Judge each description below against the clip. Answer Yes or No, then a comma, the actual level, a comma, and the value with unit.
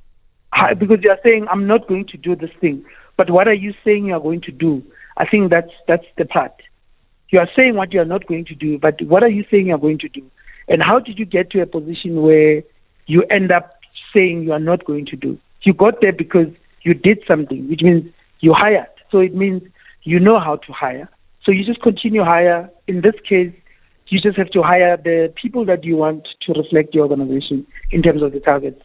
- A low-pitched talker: No, medium, 175 Hz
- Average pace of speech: No, fast, 235 wpm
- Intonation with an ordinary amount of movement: Yes, average, 4.0 semitones